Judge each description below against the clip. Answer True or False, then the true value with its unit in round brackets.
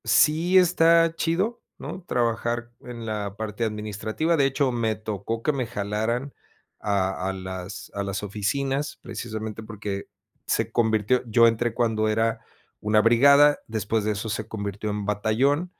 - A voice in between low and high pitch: False (110 Hz)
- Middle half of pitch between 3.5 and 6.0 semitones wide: True (4.2 semitones)